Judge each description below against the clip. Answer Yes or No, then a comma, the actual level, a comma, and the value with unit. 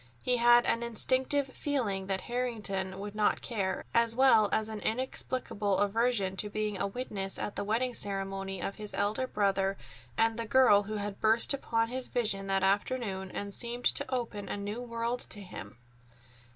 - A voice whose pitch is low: No, high, 215 Hz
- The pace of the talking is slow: No, average, 175 wpm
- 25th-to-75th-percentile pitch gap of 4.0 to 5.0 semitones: No, average, 3.4 semitones